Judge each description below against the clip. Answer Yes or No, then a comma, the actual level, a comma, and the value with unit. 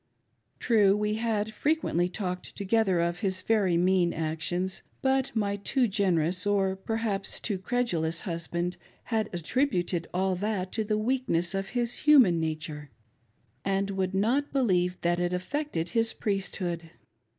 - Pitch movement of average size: Yes, average, 4.0 semitones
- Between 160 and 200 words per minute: No, average, 140 wpm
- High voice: Yes, high, 195 Hz